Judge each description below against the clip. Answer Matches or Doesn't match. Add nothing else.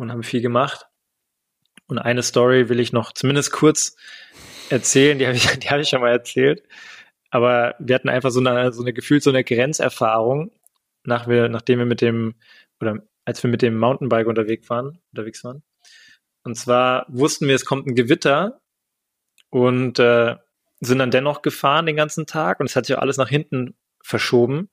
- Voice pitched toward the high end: Doesn't match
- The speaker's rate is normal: Matches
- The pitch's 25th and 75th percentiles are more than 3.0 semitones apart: Doesn't match